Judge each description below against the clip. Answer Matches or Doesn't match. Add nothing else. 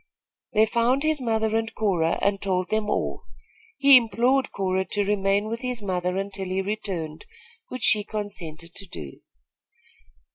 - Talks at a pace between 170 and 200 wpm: Doesn't match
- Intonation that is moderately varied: Matches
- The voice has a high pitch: Matches